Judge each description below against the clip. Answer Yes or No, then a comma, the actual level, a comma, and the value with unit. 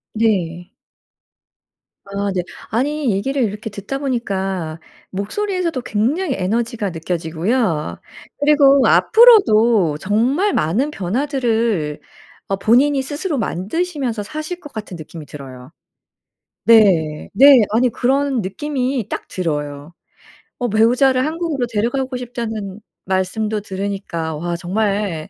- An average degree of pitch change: No, wide, 6.3 semitones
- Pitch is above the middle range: Yes, high, 220 Hz